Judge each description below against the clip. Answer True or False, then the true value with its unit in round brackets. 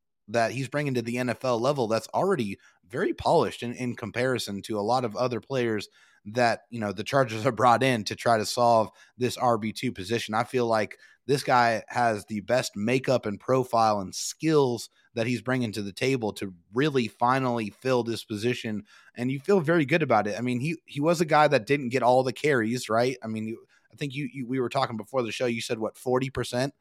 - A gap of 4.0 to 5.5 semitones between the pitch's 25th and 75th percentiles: False (2.8 semitones)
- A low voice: True (120 Hz)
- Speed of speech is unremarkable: False (225 wpm)